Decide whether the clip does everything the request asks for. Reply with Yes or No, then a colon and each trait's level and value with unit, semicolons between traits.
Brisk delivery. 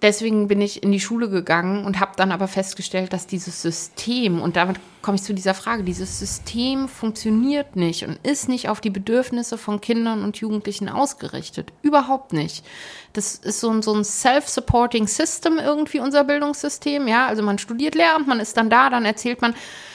No: average, 180 wpm